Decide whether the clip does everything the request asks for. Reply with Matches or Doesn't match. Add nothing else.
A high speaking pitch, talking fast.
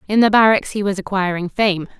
Matches